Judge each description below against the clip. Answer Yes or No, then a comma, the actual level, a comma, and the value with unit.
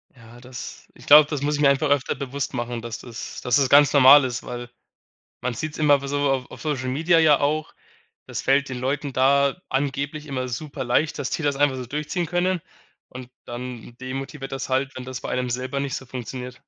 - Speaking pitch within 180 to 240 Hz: No, low, 135 Hz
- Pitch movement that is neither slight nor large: No, narrow, 2.3 semitones